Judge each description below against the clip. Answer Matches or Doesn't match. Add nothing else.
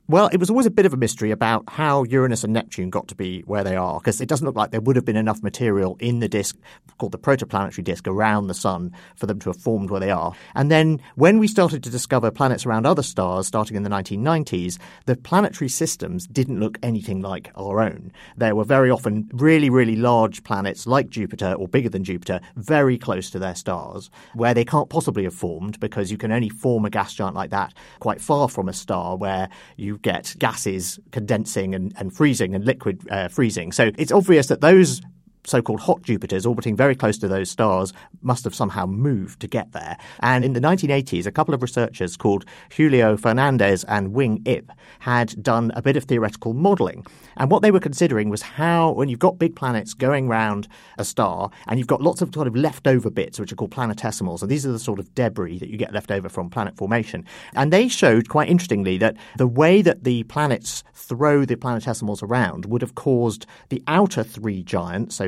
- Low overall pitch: Matches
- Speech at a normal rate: Doesn't match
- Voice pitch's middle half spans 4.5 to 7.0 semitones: Matches